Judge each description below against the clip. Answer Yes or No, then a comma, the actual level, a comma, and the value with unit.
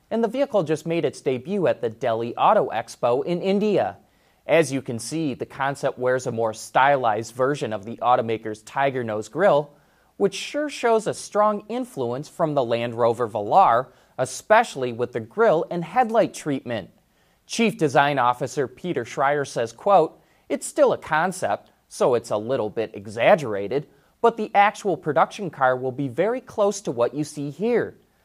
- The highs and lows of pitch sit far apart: Yes, wide, 8.5 semitones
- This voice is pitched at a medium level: Yes, medium, 145 Hz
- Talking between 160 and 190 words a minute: Yes, average, 170 wpm